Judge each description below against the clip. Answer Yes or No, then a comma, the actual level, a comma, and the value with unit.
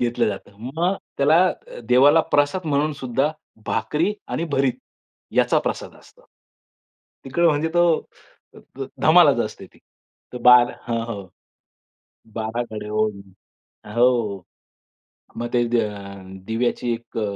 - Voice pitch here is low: Yes, low, 120 Hz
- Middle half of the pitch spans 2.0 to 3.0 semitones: No, average, 4.5 semitones